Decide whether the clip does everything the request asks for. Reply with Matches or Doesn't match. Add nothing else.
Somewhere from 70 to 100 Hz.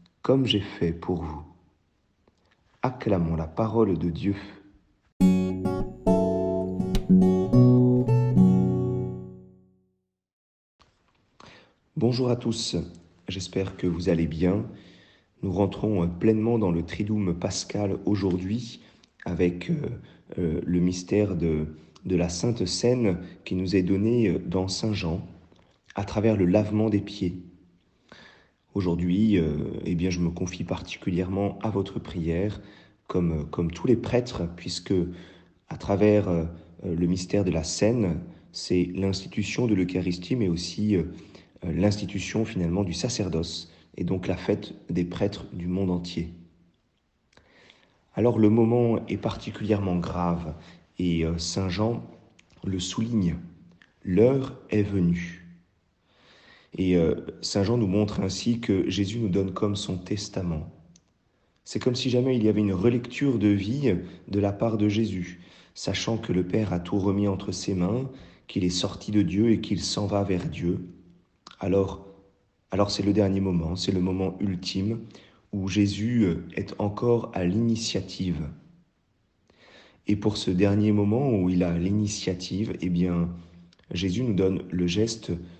Matches